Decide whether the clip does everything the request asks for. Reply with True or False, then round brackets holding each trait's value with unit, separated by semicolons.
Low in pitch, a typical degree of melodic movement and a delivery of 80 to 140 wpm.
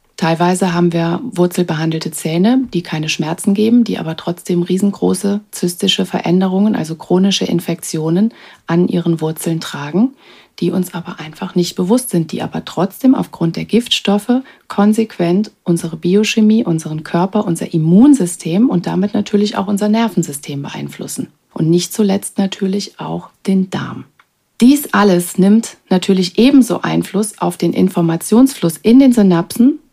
False (185 Hz; 3.8 semitones; 135 wpm)